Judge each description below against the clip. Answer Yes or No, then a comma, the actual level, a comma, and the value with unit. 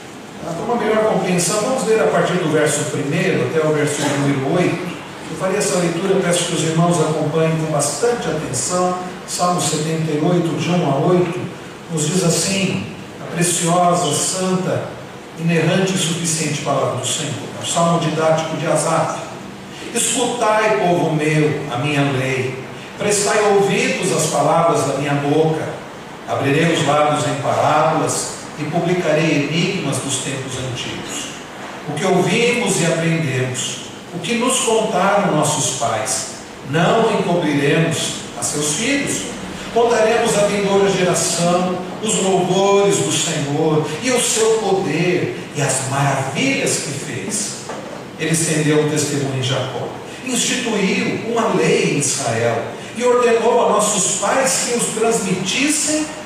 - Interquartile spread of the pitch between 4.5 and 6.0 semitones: Yes, average, 4.8 semitones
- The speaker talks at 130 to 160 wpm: Yes, average, 135 wpm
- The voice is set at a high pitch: No, medium, 170 Hz